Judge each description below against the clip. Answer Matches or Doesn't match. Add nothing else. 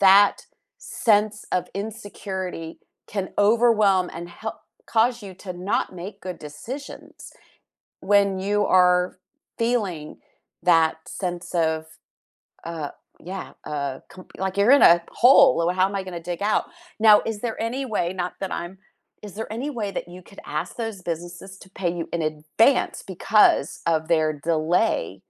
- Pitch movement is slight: Doesn't match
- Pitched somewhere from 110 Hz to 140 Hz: Doesn't match